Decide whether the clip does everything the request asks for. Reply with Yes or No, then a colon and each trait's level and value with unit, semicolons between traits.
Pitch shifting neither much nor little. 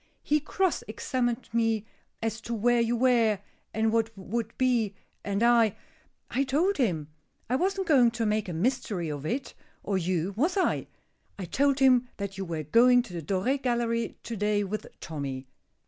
Yes: average, 4.3 semitones